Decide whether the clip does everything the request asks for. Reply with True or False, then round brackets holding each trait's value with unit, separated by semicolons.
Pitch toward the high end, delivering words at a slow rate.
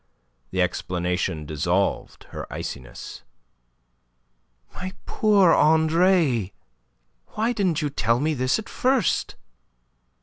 False (150 Hz; 95 wpm)